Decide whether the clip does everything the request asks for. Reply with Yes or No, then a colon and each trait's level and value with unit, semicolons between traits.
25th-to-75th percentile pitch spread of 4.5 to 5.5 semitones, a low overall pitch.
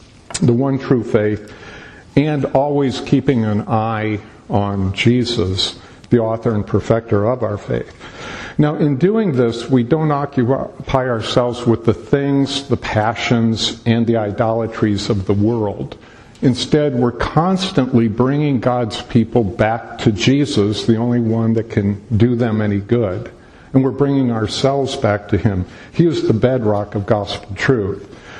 No: average, 3.8 semitones; low, 115 Hz